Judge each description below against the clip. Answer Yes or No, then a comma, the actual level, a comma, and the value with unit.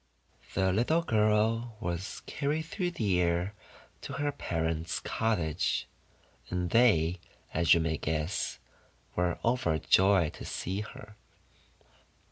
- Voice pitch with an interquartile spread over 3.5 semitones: Yes, average, 5.1 semitones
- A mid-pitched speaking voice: No, very low, 95 Hz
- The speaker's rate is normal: No, slow, 110 wpm